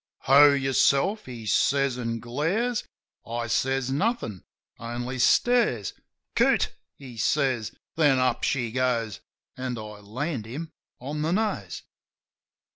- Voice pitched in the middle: No, low, 130 Hz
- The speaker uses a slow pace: Yes, slow, 130 wpm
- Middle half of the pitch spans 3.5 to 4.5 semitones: Yes, average, 3.9 semitones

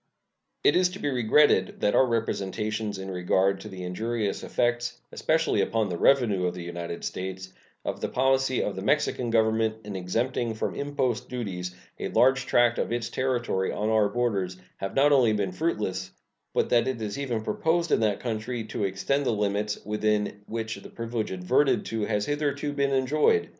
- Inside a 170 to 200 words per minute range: Yes, average, 180 wpm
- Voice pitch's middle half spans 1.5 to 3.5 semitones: No, average, 4.5 semitones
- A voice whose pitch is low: Yes, low, 110 Hz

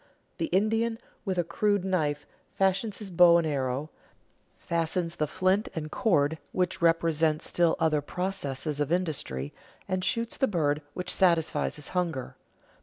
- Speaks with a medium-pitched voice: Yes, medium, 170 Hz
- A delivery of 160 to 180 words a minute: No, average, 145 wpm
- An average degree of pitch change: Yes, average, 3.6 semitones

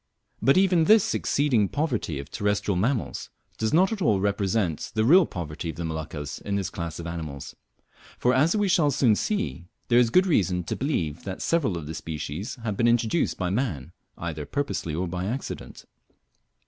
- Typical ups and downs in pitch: No, wide, 8.7 semitones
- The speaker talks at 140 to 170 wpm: No, average, 185 wpm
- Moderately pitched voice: No, low, 105 Hz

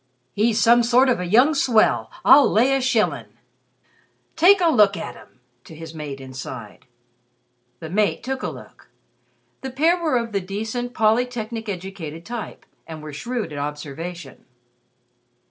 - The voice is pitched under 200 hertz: No, high, 215 Hz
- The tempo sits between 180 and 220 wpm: No, average, 150 wpm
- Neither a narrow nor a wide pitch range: No, wide, 7.4 semitones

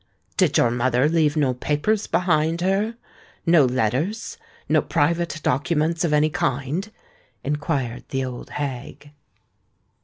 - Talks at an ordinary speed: No, slow, 110 wpm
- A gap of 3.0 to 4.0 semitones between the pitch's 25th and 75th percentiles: No, average, 4.4 semitones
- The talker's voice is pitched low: No, medium, 150 Hz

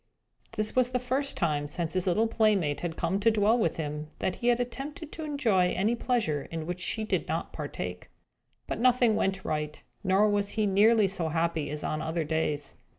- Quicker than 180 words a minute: Yes, average, 200 wpm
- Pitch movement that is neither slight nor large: No, wide, 6.1 semitones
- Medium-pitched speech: No, high, 195 Hz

